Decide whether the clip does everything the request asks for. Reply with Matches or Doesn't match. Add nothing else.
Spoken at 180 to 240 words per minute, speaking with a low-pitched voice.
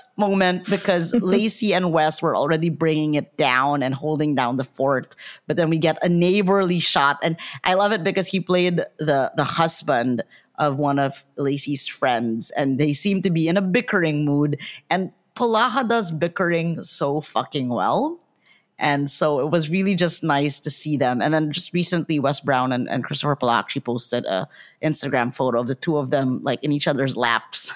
Doesn't match